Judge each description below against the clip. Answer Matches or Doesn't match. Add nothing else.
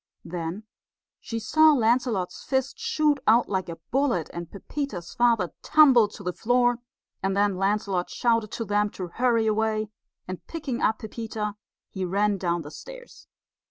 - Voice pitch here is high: Matches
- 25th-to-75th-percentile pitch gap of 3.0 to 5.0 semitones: Matches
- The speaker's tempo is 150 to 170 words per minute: Matches